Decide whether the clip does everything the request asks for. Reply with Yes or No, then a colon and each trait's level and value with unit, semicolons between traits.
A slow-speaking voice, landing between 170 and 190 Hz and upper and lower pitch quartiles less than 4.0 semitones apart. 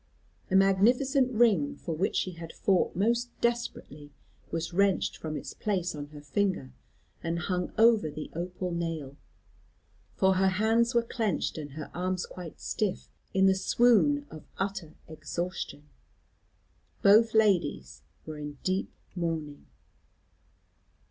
No: slow, 130 wpm; medium, 185 Hz; average, 5.0 semitones